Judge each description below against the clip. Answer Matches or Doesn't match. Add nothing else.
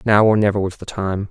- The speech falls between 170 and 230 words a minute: Doesn't match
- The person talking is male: Matches